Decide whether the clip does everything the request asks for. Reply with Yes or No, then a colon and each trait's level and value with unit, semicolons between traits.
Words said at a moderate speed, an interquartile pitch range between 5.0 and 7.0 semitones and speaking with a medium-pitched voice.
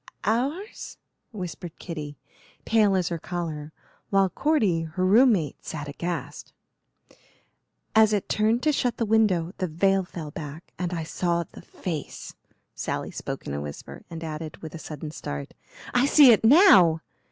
Yes: average, 155 wpm; wide, 5.5 semitones; medium, 175 Hz